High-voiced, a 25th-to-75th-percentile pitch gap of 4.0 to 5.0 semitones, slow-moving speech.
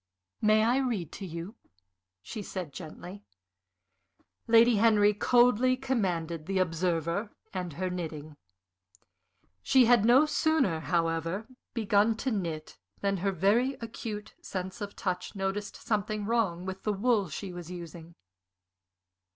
Yes: high, 200 Hz; average, 4.6 semitones; slow, 125 wpm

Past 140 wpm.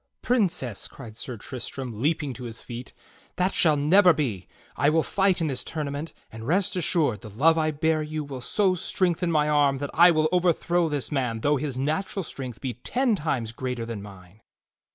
Yes: average, 190 wpm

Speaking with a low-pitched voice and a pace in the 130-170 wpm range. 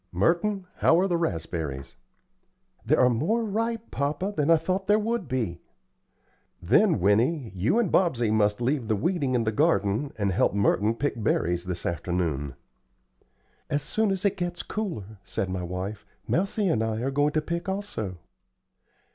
Yes: low, 130 Hz; average, 165 wpm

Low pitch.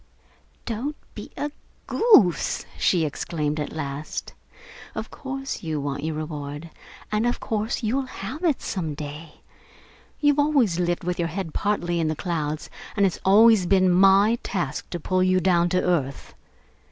No: medium, 180 Hz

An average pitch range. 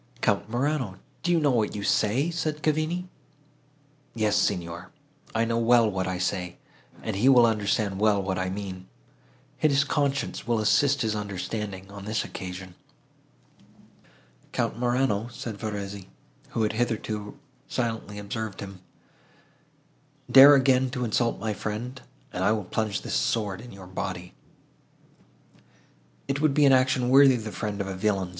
Yes: average, 4.4 semitones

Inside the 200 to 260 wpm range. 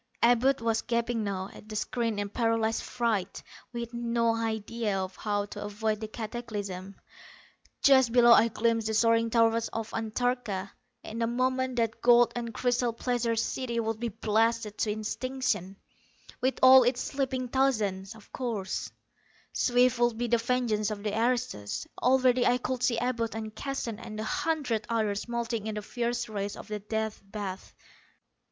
No: average, 160 wpm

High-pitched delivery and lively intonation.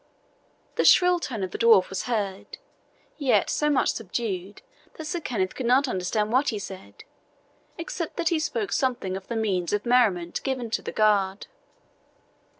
Yes: high, 225 Hz; wide, 5.8 semitones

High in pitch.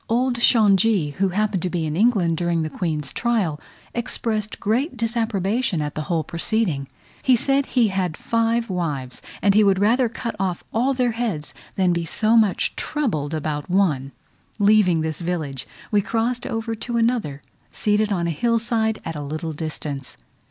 Yes: high, 200 Hz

